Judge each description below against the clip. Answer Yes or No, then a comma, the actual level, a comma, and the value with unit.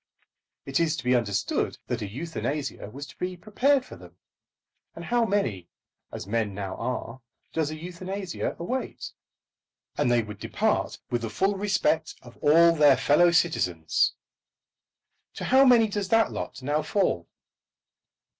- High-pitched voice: No, medium, 155 Hz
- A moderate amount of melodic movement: No, wide, 8.2 semitones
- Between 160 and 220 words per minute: No, average, 150 wpm